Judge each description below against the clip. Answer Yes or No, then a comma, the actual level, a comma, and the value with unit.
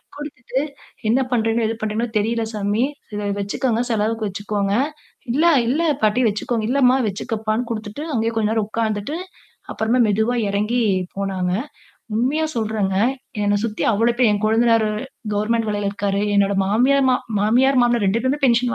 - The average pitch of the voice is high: Yes, high, 220 Hz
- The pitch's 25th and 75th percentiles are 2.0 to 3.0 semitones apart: Yes, average, 2.7 semitones